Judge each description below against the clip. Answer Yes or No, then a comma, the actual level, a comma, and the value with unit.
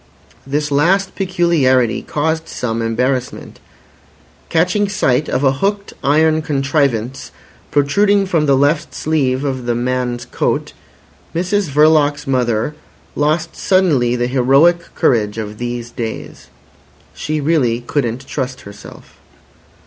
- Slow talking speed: Yes, slow, 115 wpm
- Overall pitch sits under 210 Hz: Yes, medium, 140 Hz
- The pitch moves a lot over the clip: No, average, 4.5 semitones